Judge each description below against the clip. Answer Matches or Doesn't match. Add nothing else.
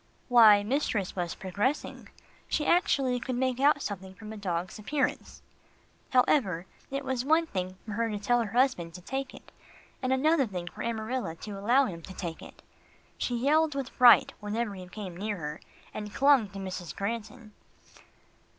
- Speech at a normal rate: Matches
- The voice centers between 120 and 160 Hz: Doesn't match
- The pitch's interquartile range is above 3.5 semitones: Matches